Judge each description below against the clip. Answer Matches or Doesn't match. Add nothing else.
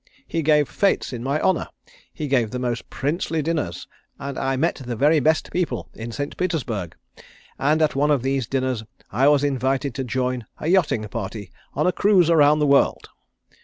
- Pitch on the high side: Doesn't match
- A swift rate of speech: Doesn't match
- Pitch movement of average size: Matches